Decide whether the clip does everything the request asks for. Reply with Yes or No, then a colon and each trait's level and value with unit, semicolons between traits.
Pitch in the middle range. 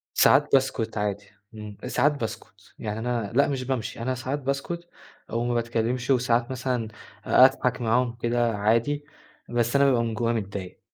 No: low, 120 Hz